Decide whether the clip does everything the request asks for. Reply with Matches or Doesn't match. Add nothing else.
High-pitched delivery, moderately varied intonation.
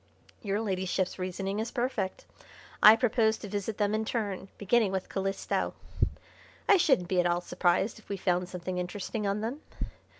Matches